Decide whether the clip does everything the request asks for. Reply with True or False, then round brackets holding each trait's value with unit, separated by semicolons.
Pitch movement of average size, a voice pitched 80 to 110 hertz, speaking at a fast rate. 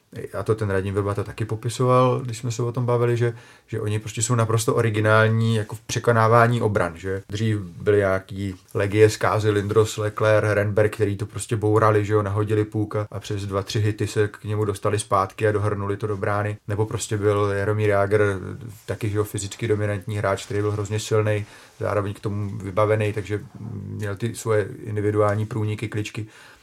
False (1.3 semitones; 105 Hz; 185 wpm)